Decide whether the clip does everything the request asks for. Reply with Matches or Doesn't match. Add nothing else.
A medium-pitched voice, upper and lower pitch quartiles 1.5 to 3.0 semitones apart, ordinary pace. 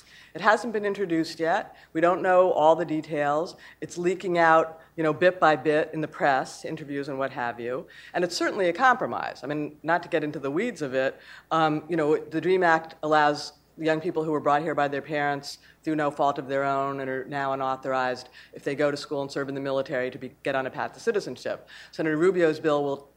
Doesn't match